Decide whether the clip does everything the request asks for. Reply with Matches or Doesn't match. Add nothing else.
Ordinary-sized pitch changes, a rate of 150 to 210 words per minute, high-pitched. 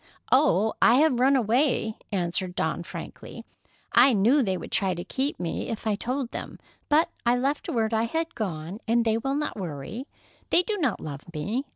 Doesn't match